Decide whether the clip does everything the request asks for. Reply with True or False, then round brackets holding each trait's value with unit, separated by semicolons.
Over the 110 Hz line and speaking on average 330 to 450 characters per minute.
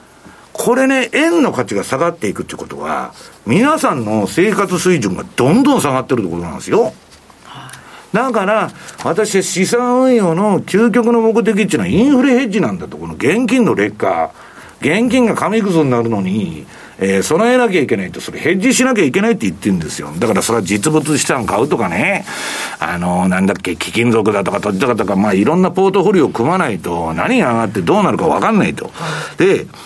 True (190 Hz; 400 characters per minute)